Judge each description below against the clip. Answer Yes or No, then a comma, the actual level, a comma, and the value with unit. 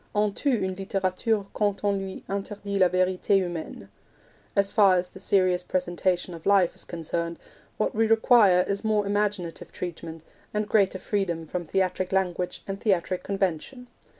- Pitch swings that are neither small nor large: No, narrow, 2.2 semitones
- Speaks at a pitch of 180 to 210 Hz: Yes, high, 190 Hz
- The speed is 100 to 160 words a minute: Yes, average, 150 wpm